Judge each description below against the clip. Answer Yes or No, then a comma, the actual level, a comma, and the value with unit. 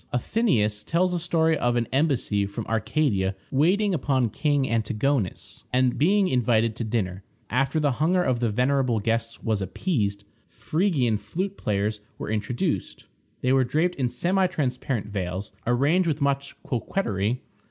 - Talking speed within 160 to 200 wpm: No, average, 145 wpm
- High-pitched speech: No, low, 125 Hz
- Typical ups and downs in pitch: No, wide, 6.2 semitones